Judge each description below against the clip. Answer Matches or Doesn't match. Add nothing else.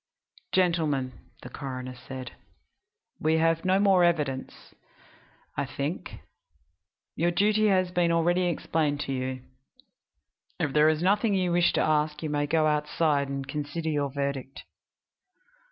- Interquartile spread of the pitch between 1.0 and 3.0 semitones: Doesn't match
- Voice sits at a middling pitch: Matches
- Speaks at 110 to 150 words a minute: Matches